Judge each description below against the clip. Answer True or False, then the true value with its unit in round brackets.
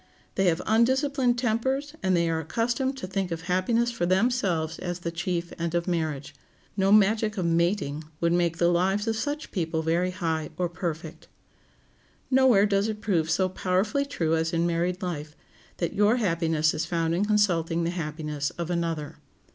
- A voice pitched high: False (180 Hz)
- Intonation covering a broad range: False (4.2 semitones)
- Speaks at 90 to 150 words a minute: False (175 wpm)